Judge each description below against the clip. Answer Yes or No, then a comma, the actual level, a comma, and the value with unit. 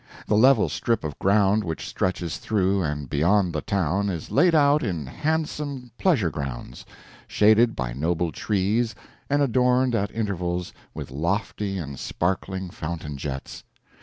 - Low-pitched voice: Yes, very low, 95 Hz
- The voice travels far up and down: Yes, wide, 6.0 semitones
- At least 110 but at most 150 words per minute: Yes, average, 140 wpm